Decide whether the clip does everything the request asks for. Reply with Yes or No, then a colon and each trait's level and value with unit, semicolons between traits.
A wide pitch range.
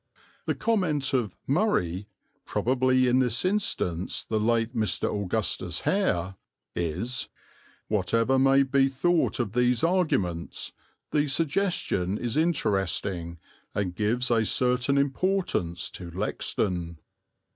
Yes: wide, 6.2 semitones